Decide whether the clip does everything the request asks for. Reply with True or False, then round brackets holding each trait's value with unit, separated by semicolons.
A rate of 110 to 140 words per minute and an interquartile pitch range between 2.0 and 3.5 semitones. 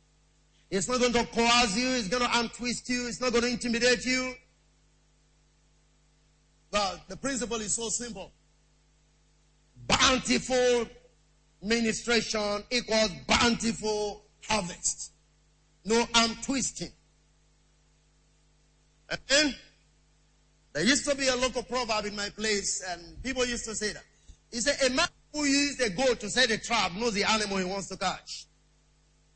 True (135 wpm; 3.1 semitones)